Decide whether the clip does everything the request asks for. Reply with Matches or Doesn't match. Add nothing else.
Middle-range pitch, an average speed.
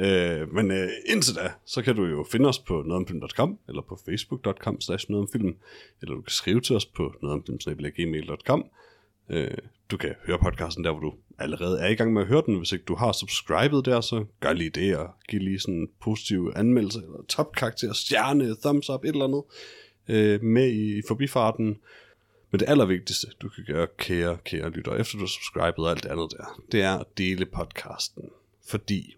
Doesn't match